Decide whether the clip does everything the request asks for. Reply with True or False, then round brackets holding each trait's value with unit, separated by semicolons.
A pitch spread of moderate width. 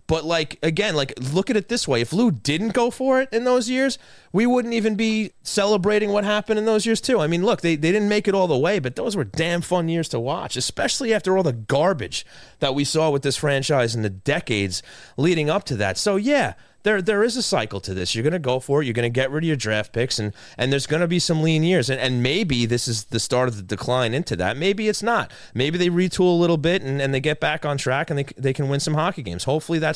False (7.7 semitones)